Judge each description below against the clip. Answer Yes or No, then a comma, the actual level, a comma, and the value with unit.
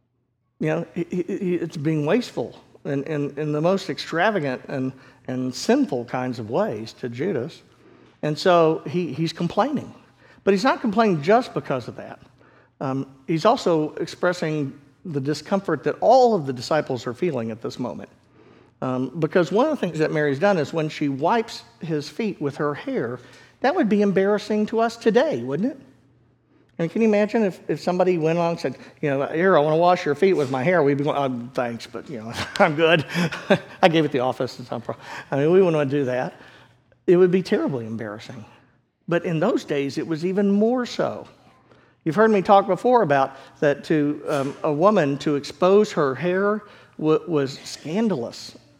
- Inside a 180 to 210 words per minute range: Yes, average, 195 wpm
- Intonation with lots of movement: Yes, wide, 6.0 semitones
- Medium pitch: Yes, medium, 155 Hz